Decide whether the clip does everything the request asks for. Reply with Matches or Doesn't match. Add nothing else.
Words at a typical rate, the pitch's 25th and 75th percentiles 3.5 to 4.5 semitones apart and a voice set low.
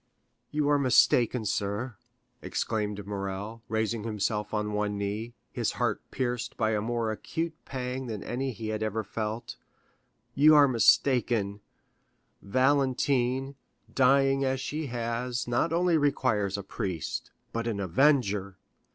Doesn't match